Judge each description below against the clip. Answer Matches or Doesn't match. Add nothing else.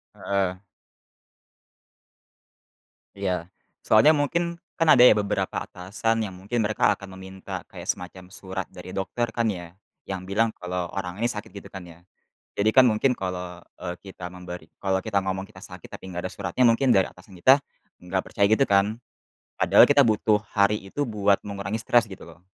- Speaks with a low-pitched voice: Matches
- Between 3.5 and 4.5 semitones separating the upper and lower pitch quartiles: Doesn't match